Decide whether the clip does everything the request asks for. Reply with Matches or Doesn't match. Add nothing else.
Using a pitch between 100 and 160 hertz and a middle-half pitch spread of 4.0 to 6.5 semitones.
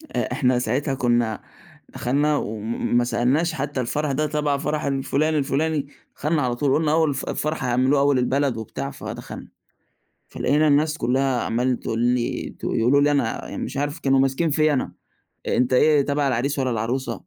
Doesn't match